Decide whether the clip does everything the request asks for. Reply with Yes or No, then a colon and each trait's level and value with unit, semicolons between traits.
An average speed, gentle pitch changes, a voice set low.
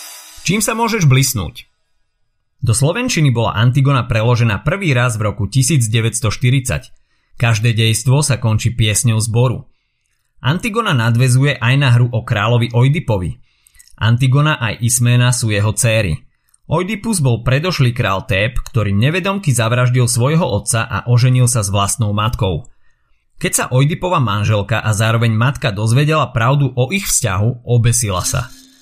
No: average, 135 wpm; average, 3.4 semitones; low, 120 Hz